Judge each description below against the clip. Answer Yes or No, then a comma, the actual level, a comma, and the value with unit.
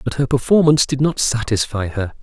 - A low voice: Yes, low, 125 Hz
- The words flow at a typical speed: Yes, average, 190 wpm